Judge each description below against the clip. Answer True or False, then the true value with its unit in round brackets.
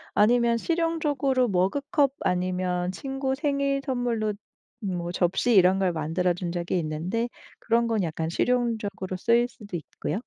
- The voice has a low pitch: False (215 Hz)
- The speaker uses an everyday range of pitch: False (5.7 semitones)